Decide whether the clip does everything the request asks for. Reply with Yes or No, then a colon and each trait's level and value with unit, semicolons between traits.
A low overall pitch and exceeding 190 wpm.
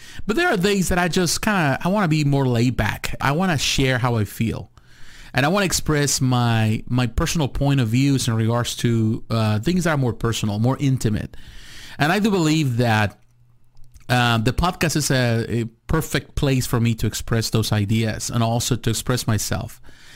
Yes: low, 125 Hz; average, 200 wpm